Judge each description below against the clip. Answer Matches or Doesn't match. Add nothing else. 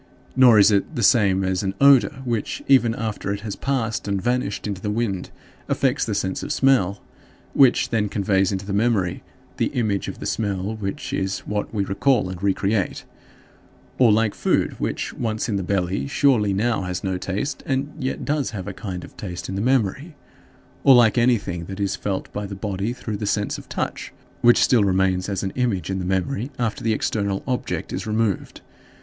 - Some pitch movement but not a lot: Matches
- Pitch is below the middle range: Matches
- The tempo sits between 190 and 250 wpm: Matches